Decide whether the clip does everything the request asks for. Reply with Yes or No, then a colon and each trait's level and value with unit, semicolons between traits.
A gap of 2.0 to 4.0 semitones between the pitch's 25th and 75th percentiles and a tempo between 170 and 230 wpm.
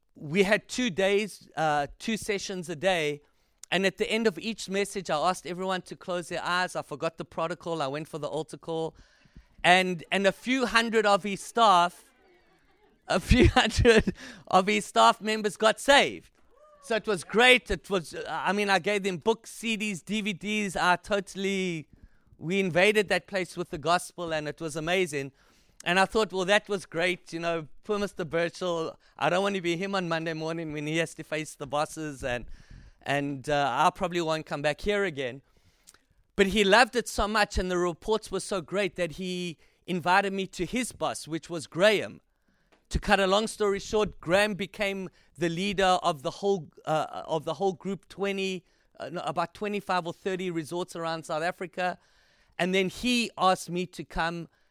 Yes: average, 3.5 semitones; average, 190 wpm